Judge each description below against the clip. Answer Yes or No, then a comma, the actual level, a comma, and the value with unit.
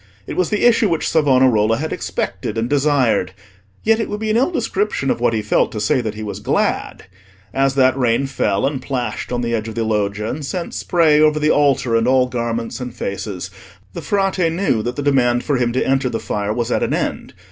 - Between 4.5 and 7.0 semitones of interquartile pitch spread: Yes, average, 5.0 semitones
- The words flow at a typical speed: No, fast, 225 wpm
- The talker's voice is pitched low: Yes, low, 130 Hz